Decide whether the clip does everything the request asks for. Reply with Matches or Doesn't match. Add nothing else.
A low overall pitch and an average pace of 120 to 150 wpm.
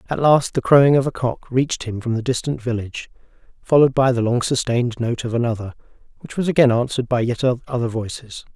Doesn't match